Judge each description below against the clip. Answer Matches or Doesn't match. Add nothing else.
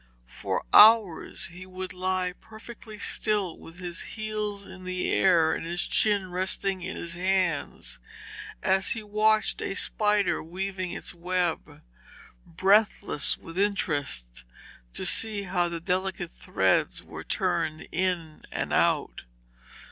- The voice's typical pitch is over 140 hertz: Matches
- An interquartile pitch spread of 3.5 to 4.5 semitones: Doesn't match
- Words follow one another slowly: Matches